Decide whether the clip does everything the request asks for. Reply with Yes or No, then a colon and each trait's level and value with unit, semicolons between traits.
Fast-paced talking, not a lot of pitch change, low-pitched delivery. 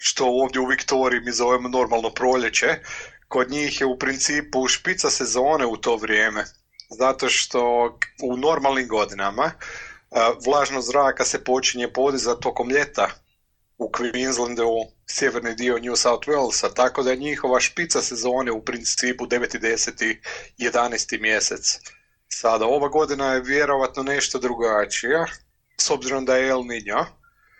No: average, 135 wpm; narrow, 2.0 semitones; low, 125 Hz